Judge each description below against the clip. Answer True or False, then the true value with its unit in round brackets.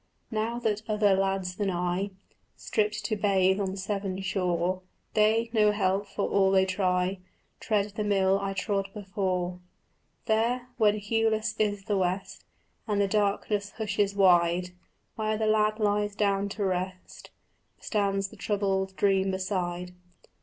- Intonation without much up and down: True (1.9 semitones)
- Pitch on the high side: True (200 Hz)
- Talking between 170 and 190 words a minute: False (140 wpm)